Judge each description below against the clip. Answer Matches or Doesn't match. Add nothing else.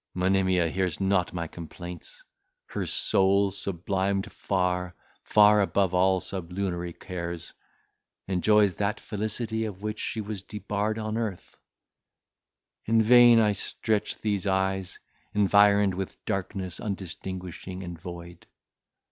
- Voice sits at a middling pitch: Doesn't match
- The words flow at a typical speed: Doesn't match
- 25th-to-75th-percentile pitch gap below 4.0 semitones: Matches